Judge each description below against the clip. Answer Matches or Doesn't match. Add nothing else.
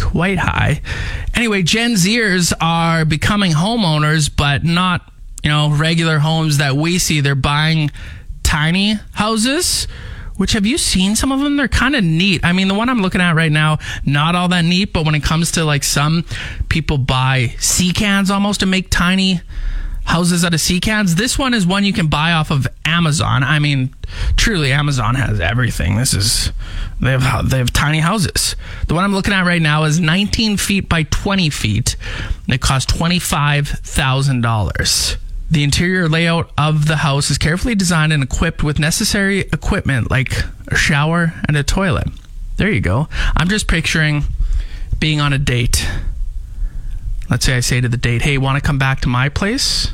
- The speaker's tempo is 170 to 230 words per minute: Matches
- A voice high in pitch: Doesn't match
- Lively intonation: Matches